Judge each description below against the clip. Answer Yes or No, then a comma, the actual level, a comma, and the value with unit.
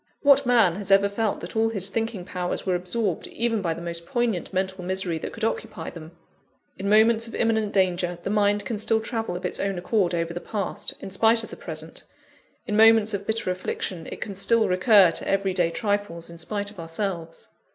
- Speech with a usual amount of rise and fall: Yes, average, 3.8 semitones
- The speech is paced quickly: Yes, fast, 210 wpm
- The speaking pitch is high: Yes, high, 200 Hz